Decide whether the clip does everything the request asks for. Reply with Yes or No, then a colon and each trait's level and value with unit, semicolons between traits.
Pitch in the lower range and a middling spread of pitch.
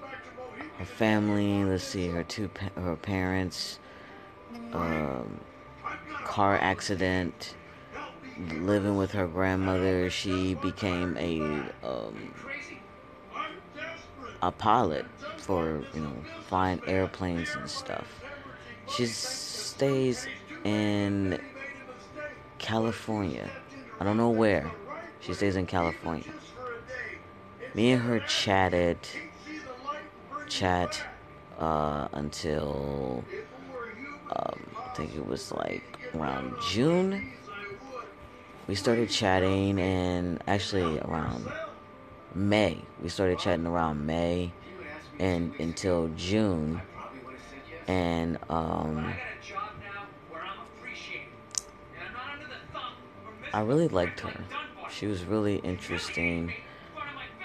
Yes: very low, 95 Hz; average, 3.4 semitones